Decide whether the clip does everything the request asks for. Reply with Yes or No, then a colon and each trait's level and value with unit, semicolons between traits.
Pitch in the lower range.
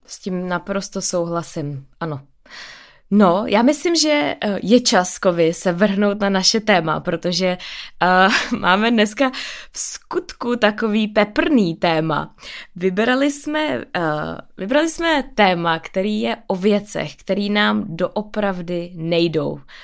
No: high, 200 Hz